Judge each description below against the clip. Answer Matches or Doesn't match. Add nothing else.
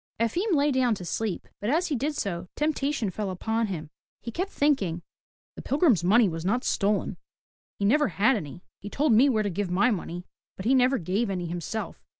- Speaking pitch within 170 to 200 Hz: Doesn't match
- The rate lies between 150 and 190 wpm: Doesn't match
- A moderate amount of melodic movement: Doesn't match